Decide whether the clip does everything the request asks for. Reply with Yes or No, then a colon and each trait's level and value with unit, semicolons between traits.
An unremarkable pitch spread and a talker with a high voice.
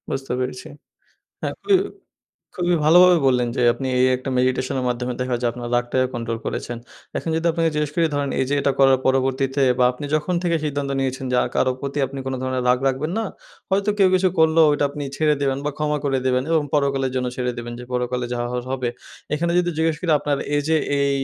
No: average, 3.2 semitones; low, 135 Hz